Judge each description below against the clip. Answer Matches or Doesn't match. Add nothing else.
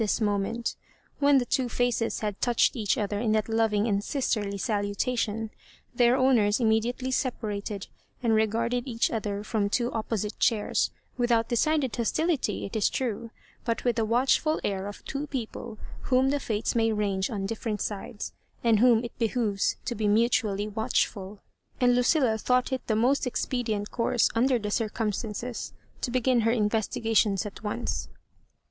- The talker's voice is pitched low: Doesn't match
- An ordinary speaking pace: Matches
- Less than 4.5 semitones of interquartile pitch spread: Matches